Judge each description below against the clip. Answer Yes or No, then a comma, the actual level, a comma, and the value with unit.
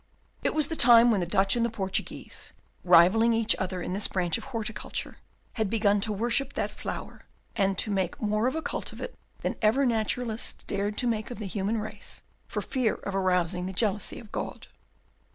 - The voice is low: No, high, 215 Hz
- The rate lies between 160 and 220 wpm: Yes, average, 200 wpm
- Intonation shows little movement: No, average, 3.3 semitones